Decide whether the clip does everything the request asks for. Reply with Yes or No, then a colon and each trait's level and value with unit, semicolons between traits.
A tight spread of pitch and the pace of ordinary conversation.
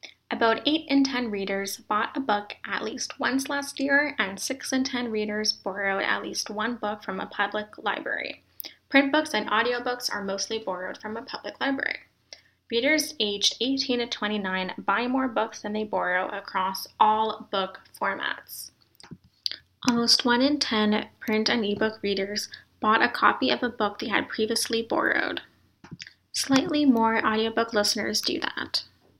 No: average, 3.2 semitones; average, 160 wpm